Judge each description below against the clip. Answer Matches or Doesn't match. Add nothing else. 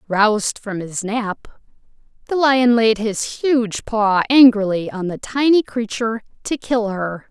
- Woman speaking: Matches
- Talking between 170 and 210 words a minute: Doesn't match